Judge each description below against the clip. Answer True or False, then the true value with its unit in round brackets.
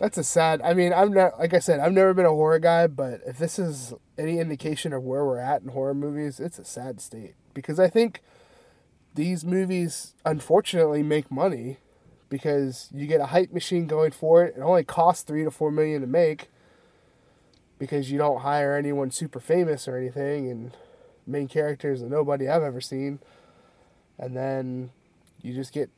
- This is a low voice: False (150 Hz)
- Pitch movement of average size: True (3.6 semitones)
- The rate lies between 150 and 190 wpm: True (185 wpm)